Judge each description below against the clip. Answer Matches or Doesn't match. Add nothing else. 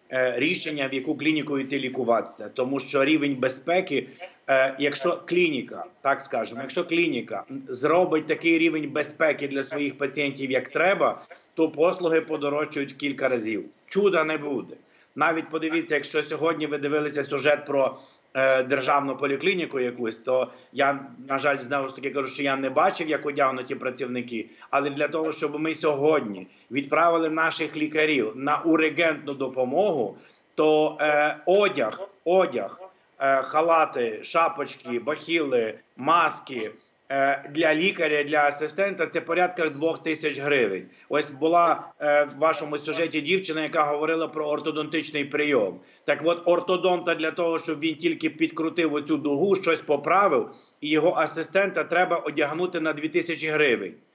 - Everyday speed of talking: Matches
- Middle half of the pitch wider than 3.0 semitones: Doesn't match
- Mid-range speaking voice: Matches